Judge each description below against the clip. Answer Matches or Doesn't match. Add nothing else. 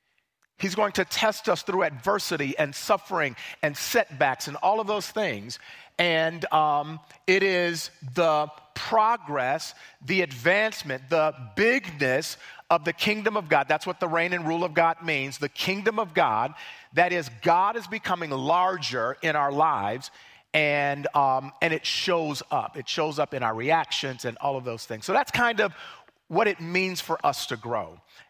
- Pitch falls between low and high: Matches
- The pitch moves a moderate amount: Matches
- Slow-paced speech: Doesn't match